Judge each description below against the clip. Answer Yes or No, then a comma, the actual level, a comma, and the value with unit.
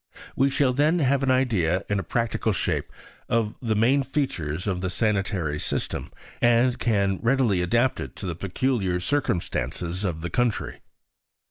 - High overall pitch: No, low, 110 Hz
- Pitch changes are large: Yes, wide, 5.9 semitones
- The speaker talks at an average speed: Yes, average, 155 wpm